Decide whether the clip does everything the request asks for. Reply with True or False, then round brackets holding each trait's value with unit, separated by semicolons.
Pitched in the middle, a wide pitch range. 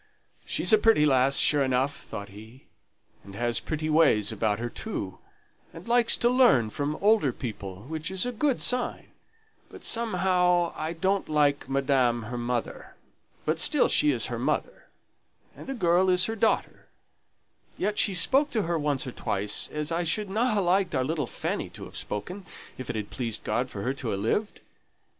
True (155 Hz; 8.2 semitones)